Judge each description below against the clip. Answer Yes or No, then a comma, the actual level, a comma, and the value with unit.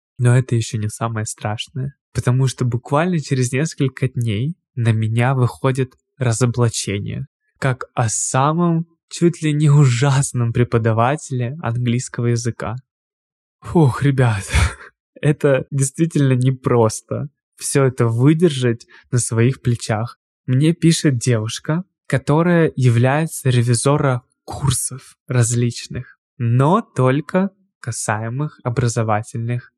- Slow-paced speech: Yes, slow, 100 wpm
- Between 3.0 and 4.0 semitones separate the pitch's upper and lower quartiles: Yes, average, 3.6 semitones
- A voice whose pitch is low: Yes, low, 130 Hz